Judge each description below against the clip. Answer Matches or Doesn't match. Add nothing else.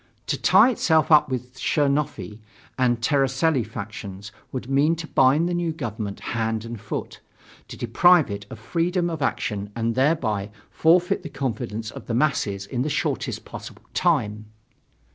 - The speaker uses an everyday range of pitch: Doesn't match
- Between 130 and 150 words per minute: Doesn't match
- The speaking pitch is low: Matches